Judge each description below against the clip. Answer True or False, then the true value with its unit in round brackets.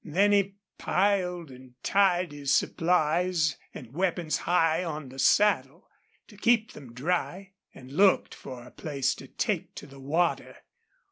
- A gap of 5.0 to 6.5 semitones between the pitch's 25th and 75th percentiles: True (5.3 semitones)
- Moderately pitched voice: True (165 Hz)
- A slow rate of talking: False (145 wpm)